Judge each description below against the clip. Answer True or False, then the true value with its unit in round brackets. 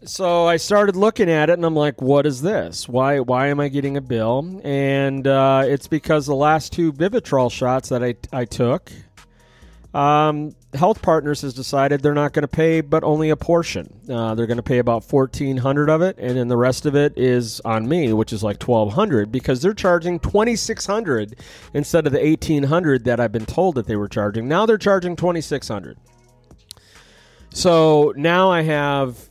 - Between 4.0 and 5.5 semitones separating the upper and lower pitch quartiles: True (4.6 semitones)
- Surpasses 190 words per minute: True (205 wpm)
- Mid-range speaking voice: True (145 Hz)